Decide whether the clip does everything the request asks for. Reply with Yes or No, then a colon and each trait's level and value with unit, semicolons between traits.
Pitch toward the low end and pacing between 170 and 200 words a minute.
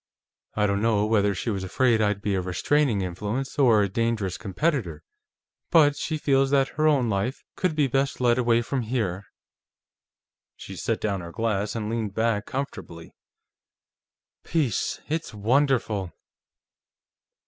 No: low, 115 Hz; average, 145 wpm